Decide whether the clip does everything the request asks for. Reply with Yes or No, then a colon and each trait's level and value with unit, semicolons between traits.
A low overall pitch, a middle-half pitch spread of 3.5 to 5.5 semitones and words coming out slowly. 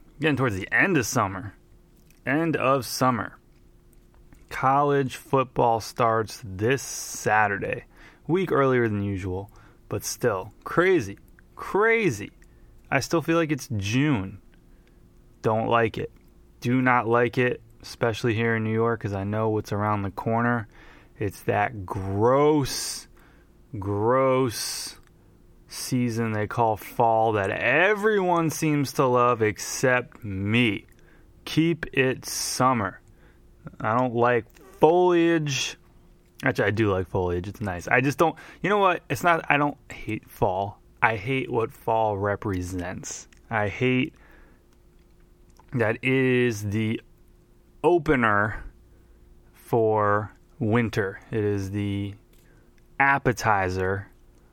Yes: low, 115 Hz; average, 4.3 semitones; slow, 115 wpm